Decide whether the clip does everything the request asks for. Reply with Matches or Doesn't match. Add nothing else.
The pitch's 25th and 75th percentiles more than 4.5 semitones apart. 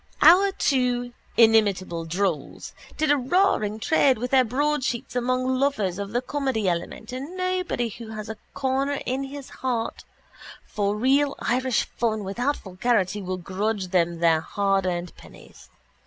Matches